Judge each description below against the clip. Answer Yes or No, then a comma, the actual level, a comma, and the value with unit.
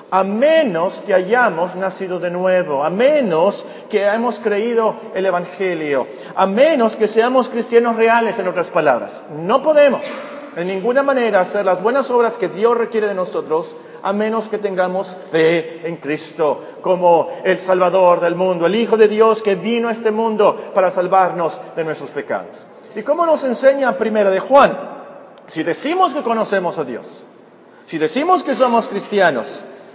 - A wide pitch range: No, average, 4.8 semitones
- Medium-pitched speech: No, high, 210 Hz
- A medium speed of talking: Yes, average, 160 wpm